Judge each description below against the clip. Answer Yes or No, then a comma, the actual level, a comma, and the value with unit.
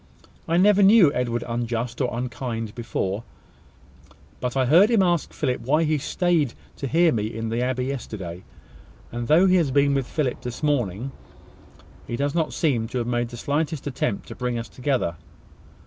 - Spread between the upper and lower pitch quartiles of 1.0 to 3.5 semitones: No, average, 4.4 semitones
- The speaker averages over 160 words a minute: Yes, average, 180 wpm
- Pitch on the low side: Yes, low, 125 Hz